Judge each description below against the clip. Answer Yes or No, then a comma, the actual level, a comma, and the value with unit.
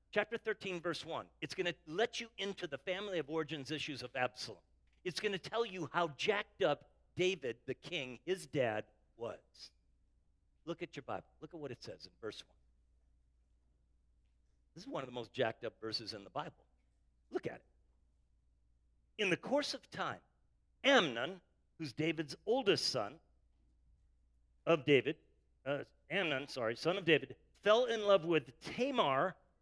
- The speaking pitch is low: No, medium, 145 Hz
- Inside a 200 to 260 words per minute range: No, average, 165 wpm